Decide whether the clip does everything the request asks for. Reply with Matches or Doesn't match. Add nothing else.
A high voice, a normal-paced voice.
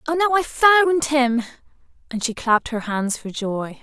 Matches